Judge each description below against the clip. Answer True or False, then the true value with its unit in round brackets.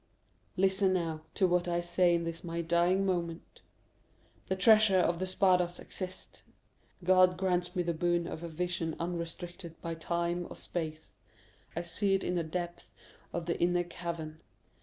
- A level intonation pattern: True (1.4 semitones)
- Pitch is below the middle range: False (175 Hz)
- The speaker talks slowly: False (160 wpm)